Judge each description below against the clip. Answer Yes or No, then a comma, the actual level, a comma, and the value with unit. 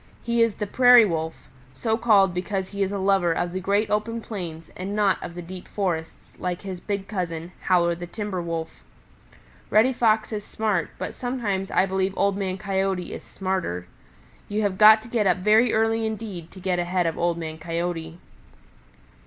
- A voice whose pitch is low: No, high, 190 Hz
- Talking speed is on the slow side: No, average, 185 wpm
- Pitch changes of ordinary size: Yes, average, 3.4 semitones